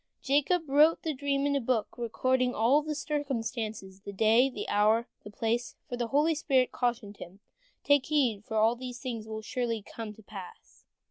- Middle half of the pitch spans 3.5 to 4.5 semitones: Yes, average, 4.2 semitones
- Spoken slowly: No, average, 180 wpm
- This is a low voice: No, high, 245 Hz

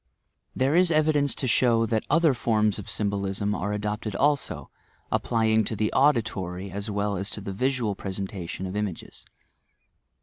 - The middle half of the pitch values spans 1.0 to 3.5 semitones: No, average, 4.2 semitones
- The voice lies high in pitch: No, low, 105 Hz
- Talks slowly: No, average, 180 wpm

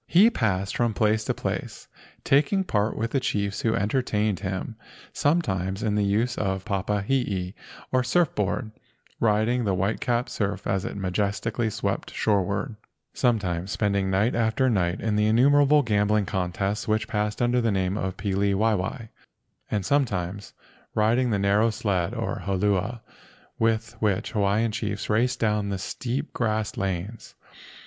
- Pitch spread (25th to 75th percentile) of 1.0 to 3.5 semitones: Yes, average, 2.8 semitones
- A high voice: No, low, 105 Hz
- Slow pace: No, average, 150 wpm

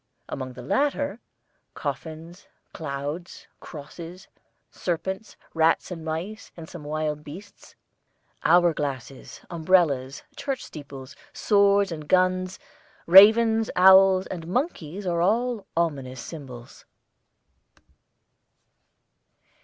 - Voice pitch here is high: No, medium, 170 Hz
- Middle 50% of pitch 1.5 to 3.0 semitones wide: No, average, 4.4 semitones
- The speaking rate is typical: No, slow, 90 wpm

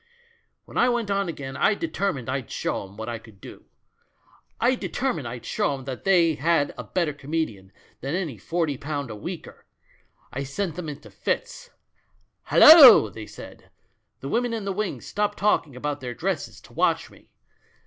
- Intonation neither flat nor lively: No, wide, 7.4 semitones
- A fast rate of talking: No, average, 170 wpm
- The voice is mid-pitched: Yes, medium, 150 Hz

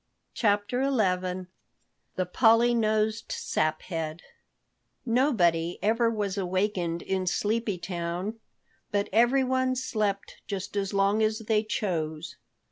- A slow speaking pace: Yes, slow, 105 wpm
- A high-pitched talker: Yes, high, 205 Hz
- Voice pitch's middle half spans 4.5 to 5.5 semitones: No, average, 3.7 semitones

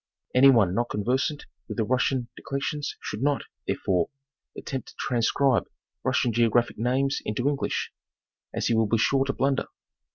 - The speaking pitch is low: Yes, low, 125 Hz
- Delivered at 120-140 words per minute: No, average, 155 wpm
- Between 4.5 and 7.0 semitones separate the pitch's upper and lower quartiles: No, average, 3.2 semitones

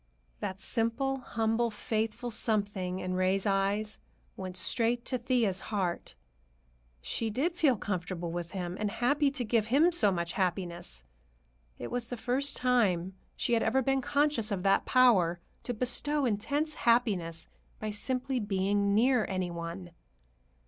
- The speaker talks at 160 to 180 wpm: No, average, 145 wpm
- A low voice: No, high, 215 Hz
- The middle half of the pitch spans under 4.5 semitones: No, average, 4.8 semitones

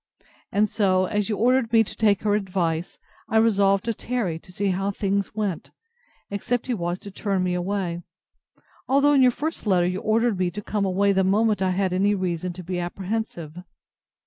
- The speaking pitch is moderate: No, high, 200 Hz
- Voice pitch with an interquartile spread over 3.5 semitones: No, average, 2.9 semitones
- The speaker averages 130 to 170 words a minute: No, average, 195 wpm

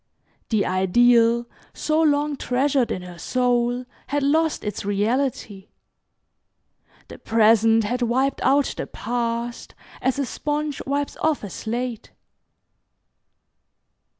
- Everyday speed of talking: No, slow, 110 wpm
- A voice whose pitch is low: No, high, 245 Hz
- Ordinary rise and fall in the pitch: Yes, average, 3.8 semitones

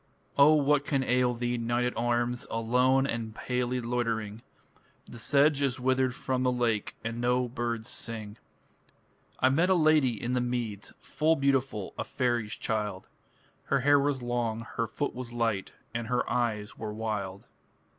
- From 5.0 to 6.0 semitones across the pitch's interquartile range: No, narrow, 2.4 semitones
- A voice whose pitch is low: Yes, low, 120 Hz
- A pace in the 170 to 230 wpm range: No, average, 160 wpm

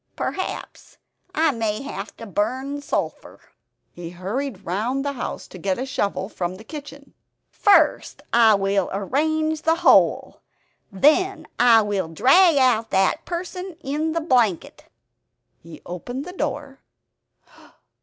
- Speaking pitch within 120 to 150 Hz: No, high, 245 Hz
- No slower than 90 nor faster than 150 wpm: Yes, slow, 135 wpm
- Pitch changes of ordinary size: No, wide, 7.5 semitones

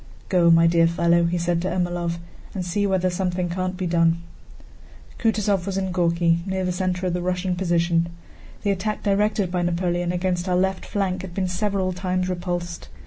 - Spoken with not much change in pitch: Yes, narrow, 1.5 semitones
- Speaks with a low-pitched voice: No, medium, 180 Hz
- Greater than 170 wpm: Yes, average, 185 wpm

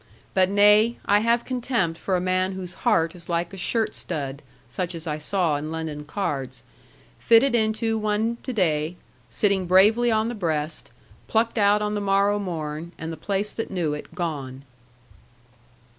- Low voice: No, medium, 185 Hz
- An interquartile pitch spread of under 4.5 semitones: No, average, 4.8 semitones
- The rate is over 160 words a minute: Yes, average, 170 wpm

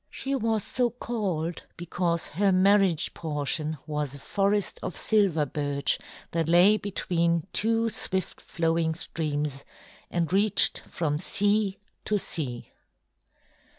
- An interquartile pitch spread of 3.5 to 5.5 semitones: Yes, average, 4.7 semitones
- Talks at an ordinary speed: No, slow, 120 wpm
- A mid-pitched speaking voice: Yes, medium, 175 Hz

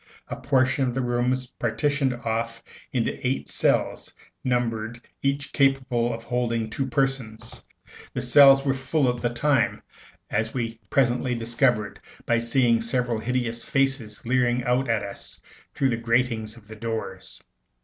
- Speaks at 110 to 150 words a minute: Yes, average, 145 wpm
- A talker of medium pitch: No, low, 120 Hz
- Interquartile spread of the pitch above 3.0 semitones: No, narrow, 2.4 semitones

